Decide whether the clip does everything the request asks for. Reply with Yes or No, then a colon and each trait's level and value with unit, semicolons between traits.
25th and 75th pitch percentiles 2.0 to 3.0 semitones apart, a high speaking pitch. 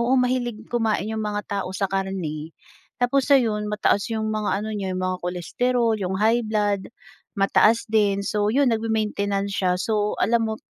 Yes: narrow, 2.5 semitones; high, 210 Hz